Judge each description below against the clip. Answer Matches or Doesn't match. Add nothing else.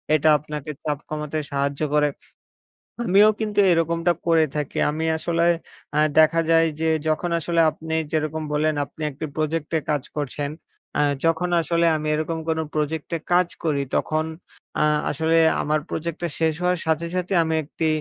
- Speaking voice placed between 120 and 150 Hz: Doesn't match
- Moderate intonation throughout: Doesn't match